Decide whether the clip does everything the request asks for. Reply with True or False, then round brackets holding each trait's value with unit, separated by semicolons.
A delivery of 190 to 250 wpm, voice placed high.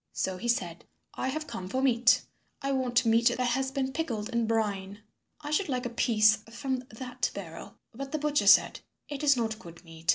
True (200 wpm; 240 Hz)